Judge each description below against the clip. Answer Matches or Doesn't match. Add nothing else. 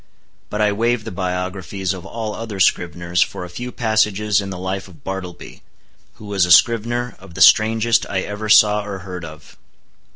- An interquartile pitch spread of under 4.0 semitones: Matches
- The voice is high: Doesn't match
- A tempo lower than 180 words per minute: Doesn't match